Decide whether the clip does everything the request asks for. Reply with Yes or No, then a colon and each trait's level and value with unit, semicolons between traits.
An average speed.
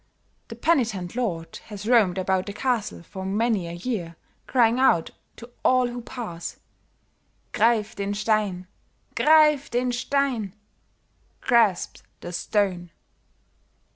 No: slow, 115 wpm